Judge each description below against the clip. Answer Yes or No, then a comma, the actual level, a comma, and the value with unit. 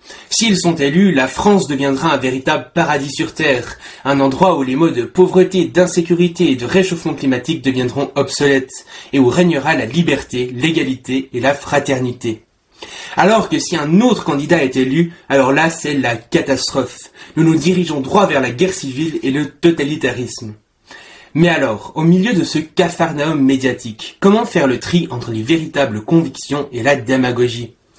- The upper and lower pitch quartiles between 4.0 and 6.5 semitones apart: Yes, average, 4.5 semitones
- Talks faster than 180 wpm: No, average, 165 wpm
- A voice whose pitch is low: No, medium, 145 Hz